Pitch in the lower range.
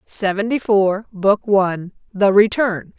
No: high, 200 Hz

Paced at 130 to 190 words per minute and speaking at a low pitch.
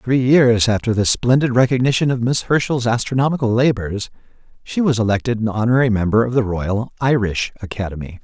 Yes: average, 160 wpm; low, 120 Hz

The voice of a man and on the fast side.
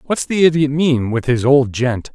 No: male; average, 195 wpm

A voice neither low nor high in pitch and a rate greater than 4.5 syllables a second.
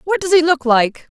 No: very high, 305 Hz; 5.0 syllables/s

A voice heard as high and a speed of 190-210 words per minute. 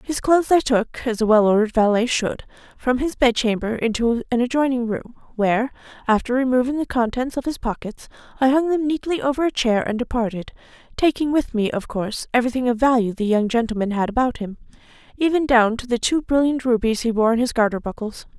Yes: high, 245 Hz; average, 200 wpm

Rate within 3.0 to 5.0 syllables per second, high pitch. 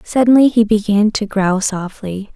Yes: 4.5 syllables/s; high, 210 Hz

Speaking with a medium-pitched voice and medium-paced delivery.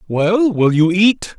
Yes: medium, 180 Hz; average, 175 wpm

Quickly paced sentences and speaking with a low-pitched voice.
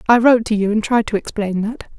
No: fast, 270 wpm; high, 220 Hz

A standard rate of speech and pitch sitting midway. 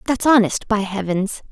No: average, 160 wpm; high, 210 Hz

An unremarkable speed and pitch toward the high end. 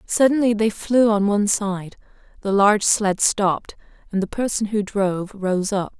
Yes: average, 170 wpm; high, 205 Hz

